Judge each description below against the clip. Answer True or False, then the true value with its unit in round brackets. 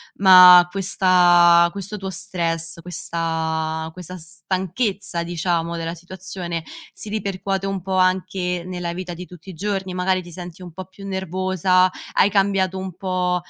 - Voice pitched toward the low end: False (185 Hz)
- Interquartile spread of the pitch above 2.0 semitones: False (1.7 semitones)